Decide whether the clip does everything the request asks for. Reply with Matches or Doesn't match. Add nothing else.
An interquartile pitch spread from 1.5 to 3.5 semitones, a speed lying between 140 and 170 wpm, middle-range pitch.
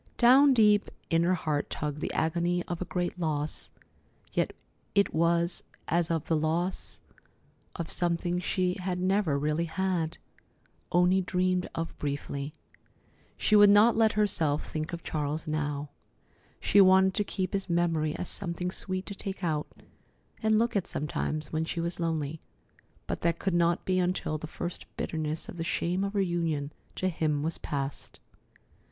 Matches